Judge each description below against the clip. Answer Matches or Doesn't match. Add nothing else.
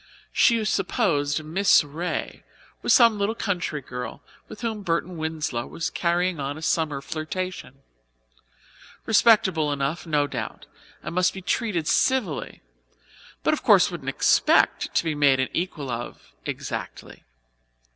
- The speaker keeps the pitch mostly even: Doesn't match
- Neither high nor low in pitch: Matches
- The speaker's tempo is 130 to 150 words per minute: Matches